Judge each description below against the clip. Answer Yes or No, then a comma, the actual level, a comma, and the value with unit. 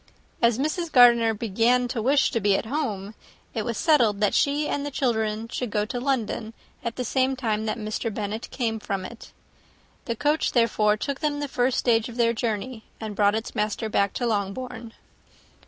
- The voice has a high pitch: Yes, high, 230 Hz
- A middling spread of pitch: Yes, average, 3.2 semitones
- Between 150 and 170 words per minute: No, average, 190 wpm